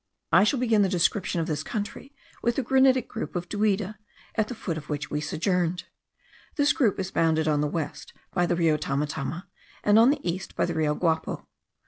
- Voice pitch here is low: No, medium, 180 Hz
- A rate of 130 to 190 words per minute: No, average, 200 wpm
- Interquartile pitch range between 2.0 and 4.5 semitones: No, average, 5.2 semitones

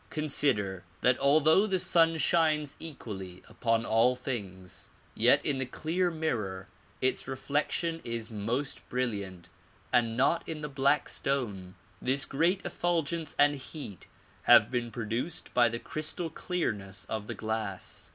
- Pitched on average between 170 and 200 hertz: No, low, 130 Hz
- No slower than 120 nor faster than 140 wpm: Yes, slow, 135 wpm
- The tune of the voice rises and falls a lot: Yes, wide, 6.1 semitones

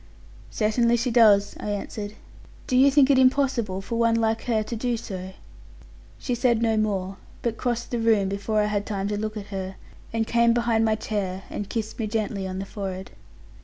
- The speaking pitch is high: Yes, high, 220 Hz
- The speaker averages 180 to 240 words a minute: Yes, average, 200 wpm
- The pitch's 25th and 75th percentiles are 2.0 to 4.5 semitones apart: Yes, average, 2.7 semitones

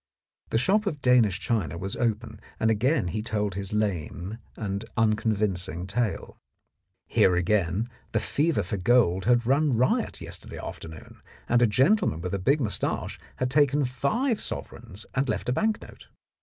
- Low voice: Yes, low, 110 Hz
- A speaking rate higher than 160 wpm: No, average, 155 wpm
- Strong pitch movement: No, average, 4.7 semitones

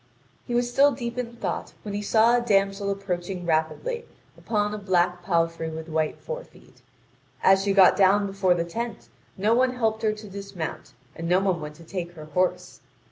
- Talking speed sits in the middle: Yes, average, 190 wpm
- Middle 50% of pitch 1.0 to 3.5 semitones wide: No, average, 4.3 semitones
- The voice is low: No, high, 195 Hz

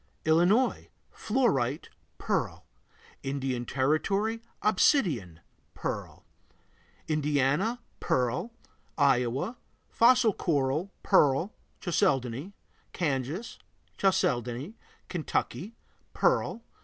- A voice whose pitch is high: No, medium, 155 Hz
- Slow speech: Yes, slow, 65 wpm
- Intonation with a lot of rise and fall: Yes, wide, 8.0 semitones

